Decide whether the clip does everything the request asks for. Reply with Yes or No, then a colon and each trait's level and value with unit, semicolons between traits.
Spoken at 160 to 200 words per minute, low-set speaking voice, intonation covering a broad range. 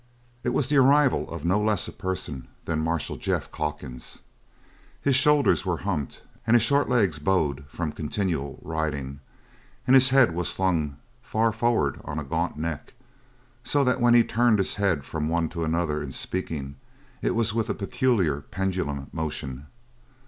Yes: average, 165 wpm; very low, 85 Hz; wide, 7.0 semitones